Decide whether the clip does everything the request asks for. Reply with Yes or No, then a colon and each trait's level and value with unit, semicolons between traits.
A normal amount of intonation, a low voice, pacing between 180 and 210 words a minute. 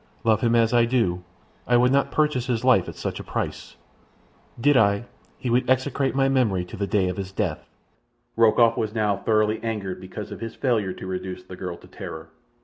Yes: average, 4.2 semitones; low, 115 Hz; fast, 205 wpm